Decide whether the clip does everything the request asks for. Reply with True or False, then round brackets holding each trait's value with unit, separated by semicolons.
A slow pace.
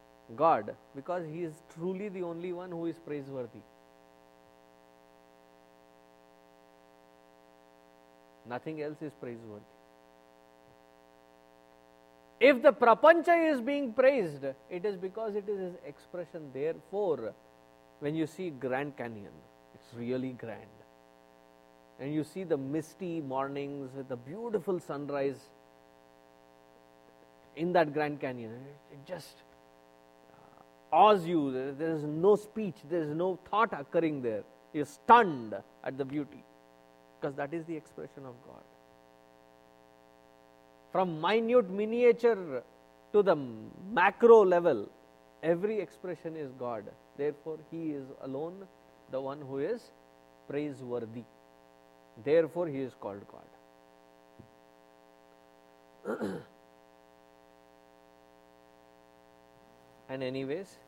True (105 wpm)